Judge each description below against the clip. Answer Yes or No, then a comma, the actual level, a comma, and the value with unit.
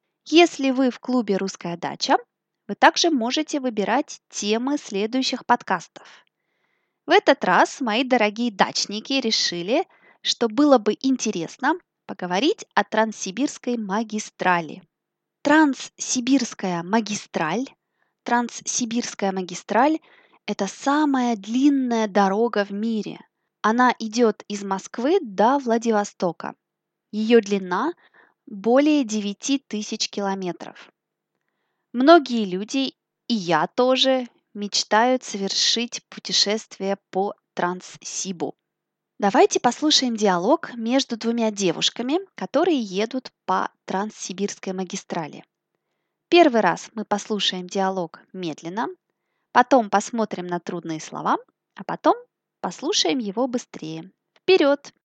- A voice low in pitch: No, high, 230 Hz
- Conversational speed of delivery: No, slow, 95 wpm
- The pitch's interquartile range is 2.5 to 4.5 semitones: No, average, 5.2 semitones